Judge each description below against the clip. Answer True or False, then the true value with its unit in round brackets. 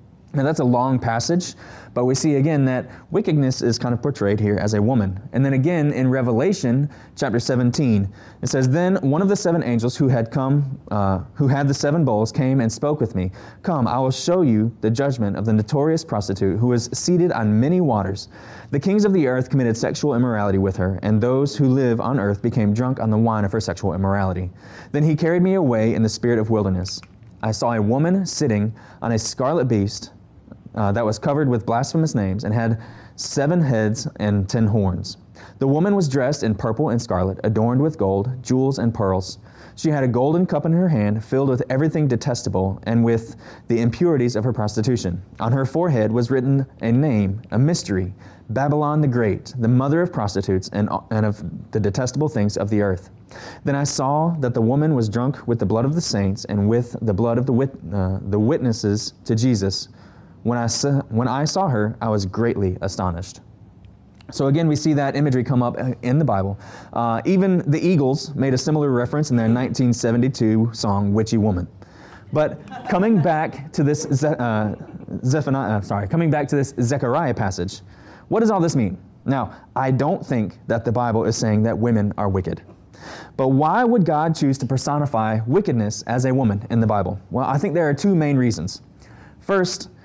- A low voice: True (120 Hz)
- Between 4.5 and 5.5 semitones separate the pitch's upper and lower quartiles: True (5.0 semitones)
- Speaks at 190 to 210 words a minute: True (200 wpm)